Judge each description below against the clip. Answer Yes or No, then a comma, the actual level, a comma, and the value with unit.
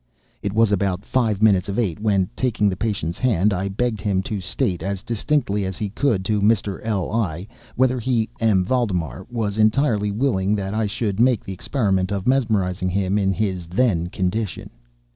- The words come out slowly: No, average, 180 wpm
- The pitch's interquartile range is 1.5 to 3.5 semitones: Yes, average, 3.0 semitones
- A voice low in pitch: Yes, low, 100 Hz